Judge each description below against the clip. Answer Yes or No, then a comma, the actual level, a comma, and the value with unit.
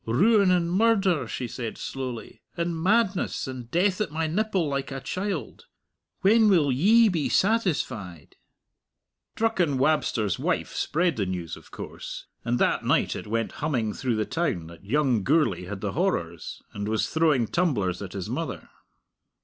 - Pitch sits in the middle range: Yes, medium, 150 Hz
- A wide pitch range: Yes, wide, 8.6 semitones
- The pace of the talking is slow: No, average, 155 wpm